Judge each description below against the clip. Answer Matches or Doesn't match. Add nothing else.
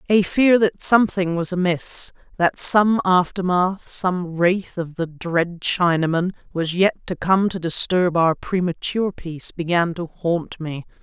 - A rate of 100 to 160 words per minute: Matches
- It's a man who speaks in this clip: Doesn't match